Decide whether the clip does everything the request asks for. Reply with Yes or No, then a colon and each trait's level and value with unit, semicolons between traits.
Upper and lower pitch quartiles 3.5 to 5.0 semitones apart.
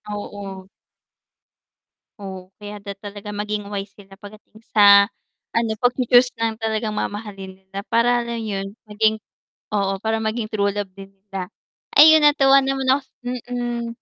No: average, 2.7 semitones